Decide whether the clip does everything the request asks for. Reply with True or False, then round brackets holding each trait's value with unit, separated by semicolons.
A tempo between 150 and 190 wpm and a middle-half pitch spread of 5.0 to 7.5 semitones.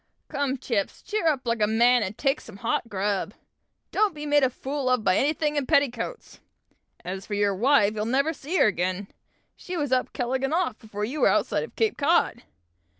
False (205 wpm; 5.6 semitones)